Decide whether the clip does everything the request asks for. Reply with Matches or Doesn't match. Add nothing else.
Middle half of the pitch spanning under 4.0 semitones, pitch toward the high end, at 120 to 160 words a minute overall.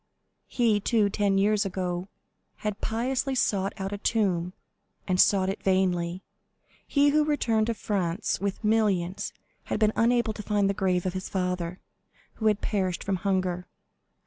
Matches